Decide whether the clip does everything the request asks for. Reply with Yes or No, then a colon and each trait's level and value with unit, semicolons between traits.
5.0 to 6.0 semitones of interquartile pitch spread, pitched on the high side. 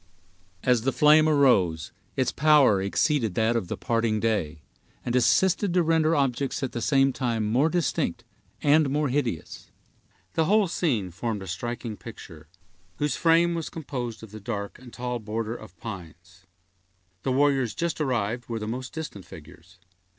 No: wide, 5.5 semitones; low, 120 Hz